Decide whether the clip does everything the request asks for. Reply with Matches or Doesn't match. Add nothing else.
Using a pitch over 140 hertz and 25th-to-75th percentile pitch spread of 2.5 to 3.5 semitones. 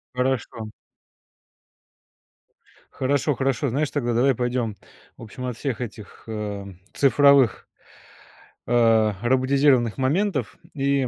Doesn't match